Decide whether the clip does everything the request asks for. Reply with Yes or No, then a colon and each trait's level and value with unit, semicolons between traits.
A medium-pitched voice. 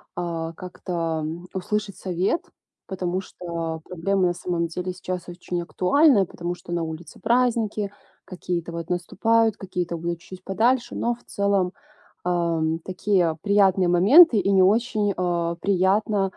Yes: medium, 180 Hz